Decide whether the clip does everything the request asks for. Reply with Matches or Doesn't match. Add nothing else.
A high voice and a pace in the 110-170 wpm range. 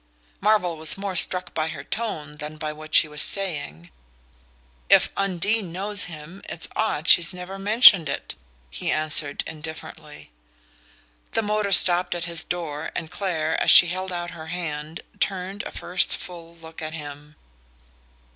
Doesn't match